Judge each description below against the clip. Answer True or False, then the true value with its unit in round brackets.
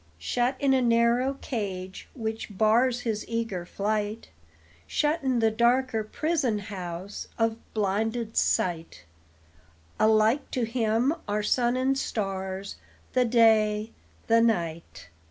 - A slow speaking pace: True (120 wpm)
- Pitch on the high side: True (225 Hz)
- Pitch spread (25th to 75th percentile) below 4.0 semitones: True (3.0 semitones)